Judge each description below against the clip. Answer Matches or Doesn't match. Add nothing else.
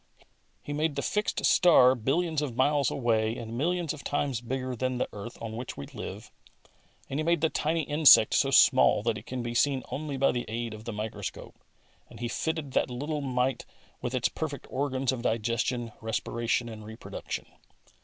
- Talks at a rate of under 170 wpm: Doesn't match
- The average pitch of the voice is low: Matches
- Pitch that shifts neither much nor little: Matches